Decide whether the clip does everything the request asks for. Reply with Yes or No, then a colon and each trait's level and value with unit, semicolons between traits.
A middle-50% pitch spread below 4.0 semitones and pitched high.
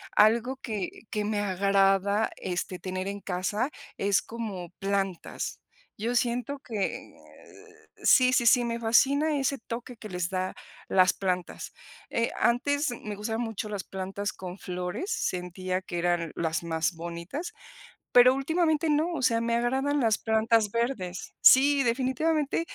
No: average, 5.3 semitones; high, 220 Hz